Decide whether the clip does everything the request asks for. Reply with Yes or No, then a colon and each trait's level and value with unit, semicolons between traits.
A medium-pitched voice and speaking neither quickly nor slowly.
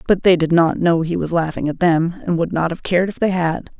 No: medium, 170 Hz; fast, 285 wpm